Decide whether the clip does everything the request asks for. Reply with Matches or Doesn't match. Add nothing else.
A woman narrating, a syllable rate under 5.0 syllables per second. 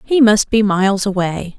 Matches